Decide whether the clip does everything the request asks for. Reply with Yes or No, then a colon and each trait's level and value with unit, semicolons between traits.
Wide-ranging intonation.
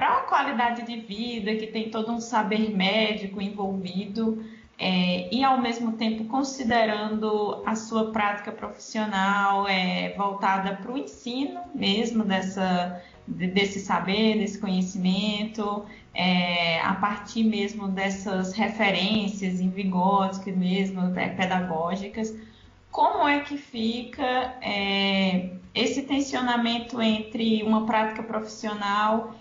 No: narrow, 2.6 semitones